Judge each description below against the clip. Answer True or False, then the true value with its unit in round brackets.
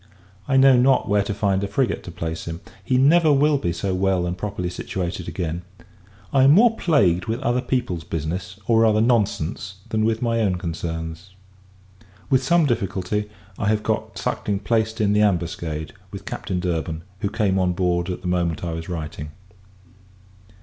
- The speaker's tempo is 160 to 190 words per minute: True (175 wpm)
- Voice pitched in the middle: False (95 Hz)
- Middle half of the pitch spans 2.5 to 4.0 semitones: False (4.6 semitones)